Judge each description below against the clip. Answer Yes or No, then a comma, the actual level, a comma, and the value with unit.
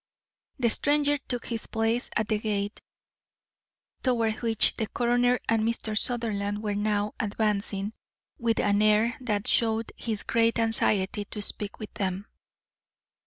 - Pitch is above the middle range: Yes, high, 220 Hz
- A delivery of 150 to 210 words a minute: No, slow, 135 wpm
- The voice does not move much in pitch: Yes, narrow, 2.0 semitones